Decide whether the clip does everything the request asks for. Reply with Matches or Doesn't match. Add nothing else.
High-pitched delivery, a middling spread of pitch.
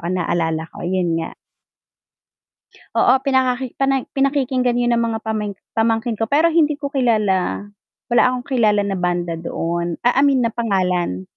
Doesn't match